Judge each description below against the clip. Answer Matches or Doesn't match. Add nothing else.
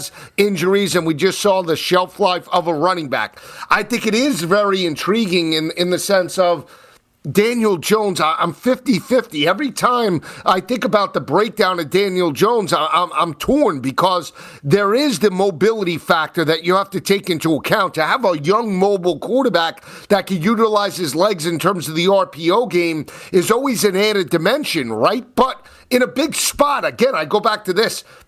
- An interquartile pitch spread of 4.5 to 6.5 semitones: Doesn't match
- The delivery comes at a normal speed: Matches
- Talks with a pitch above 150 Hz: Matches